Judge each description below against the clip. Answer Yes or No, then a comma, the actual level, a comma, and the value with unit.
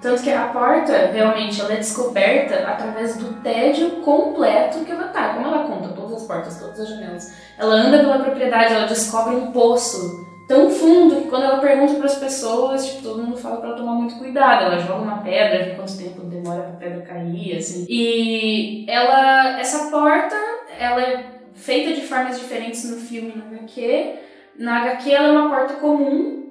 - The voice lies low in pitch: No, high, 245 Hz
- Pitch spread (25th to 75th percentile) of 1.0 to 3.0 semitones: No, average, 4.4 semitones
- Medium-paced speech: No, fast, 190 wpm